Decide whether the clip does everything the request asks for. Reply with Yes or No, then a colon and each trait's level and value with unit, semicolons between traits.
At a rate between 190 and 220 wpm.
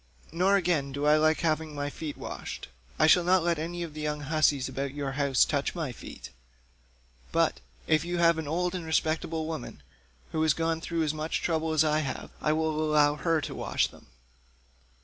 Yes: average, 200 wpm